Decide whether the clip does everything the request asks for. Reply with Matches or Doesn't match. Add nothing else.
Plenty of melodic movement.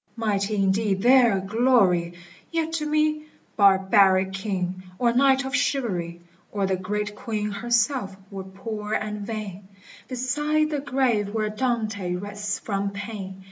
Doesn't match